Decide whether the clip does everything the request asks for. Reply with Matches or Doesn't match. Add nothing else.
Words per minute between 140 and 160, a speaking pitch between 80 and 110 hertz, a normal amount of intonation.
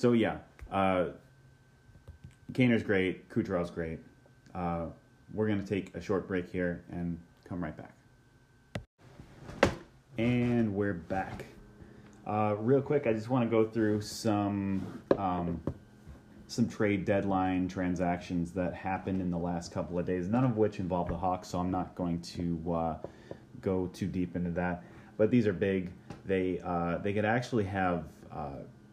Matches